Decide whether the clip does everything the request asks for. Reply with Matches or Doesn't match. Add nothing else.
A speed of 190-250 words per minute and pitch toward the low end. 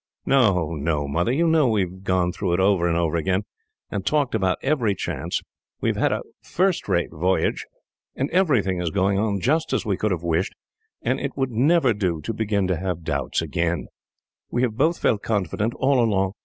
Matches